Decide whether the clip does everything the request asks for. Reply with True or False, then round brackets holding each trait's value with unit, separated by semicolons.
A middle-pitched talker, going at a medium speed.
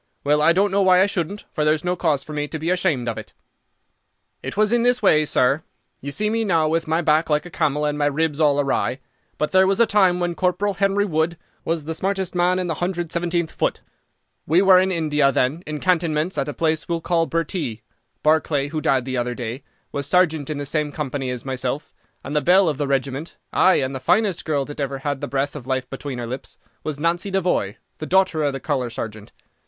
False (155 Hz; 230 wpm)